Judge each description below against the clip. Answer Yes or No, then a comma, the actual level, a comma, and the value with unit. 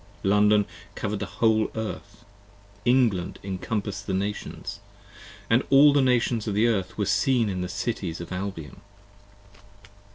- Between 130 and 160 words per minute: Yes, slow, 135 wpm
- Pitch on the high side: No, low, 105 Hz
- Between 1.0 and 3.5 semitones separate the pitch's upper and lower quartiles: Yes, average, 3.0 semitones